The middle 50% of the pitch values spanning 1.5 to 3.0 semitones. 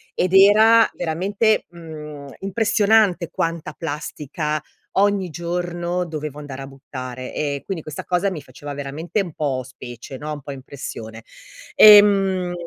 No: average, 4.9 semitones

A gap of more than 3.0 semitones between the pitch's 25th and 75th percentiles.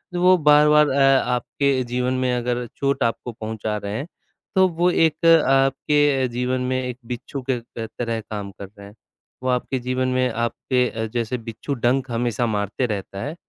No: average, 2.7 semitones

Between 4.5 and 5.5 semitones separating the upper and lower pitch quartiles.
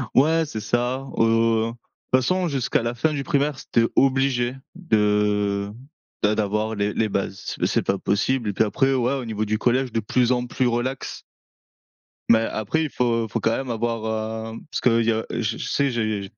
No: average, 3.2 semitones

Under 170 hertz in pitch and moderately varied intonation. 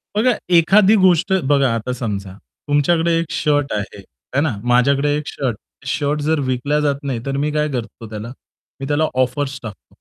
Yes: medium, 140 Hz; average, 3.3 semitones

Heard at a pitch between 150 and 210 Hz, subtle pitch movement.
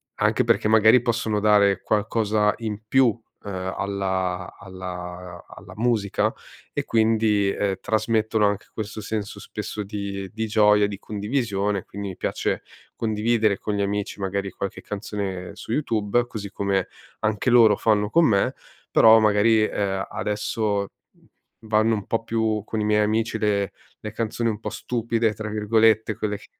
No: low, 105 Hz; narrow, 1.8 semitones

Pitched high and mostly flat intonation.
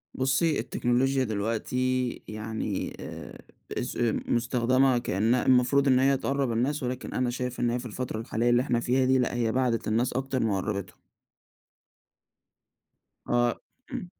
No: low, 125 Hz; narrow, 2.1 semitones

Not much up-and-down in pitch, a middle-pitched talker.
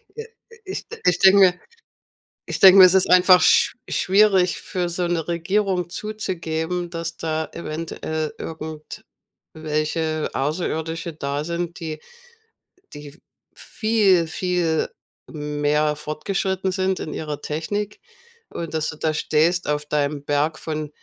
No: average, 3.0 semitones; medium, 165 Hz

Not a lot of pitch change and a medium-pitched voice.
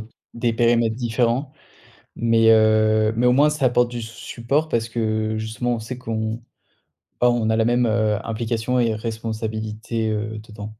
No: narrow, 1.6 semitones; low, 115 Hz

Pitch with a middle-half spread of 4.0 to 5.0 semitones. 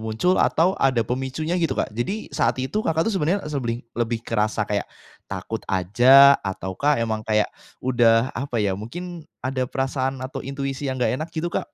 Yes: average, 4.6 semitones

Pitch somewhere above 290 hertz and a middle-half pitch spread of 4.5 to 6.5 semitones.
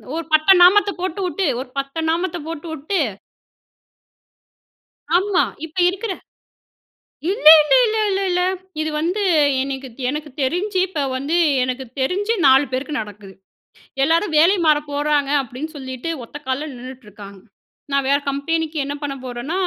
Yes: very high, 305 Hz; average, 5.0 semitones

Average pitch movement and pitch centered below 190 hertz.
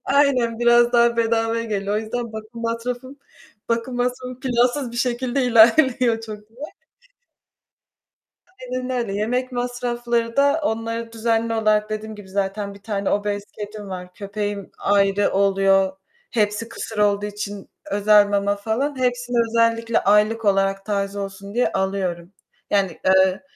No: average, 3.0 semitones; high, 220 Hz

